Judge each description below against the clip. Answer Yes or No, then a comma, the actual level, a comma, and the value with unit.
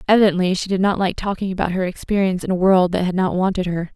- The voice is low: No, medium, 185 Hz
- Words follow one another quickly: Yes, fast, 260 wpm